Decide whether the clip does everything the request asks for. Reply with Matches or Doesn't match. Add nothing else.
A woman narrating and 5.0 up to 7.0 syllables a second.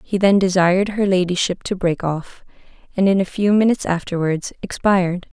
Matches